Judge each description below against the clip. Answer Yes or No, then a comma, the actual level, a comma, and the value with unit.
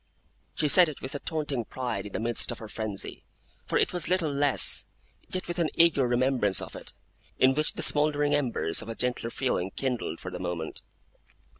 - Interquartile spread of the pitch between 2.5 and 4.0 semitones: No, average, 4.8 semitones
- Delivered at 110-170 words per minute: No, average, 195 wpm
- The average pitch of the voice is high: No, low, 130 Hz